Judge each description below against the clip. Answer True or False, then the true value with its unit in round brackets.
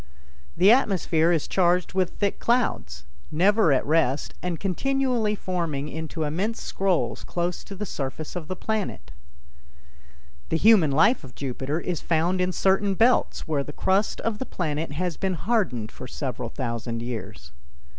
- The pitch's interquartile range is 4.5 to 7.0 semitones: True (5.6 semitones)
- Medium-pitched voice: True (175 Hz)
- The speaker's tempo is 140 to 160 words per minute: True (155 wpm)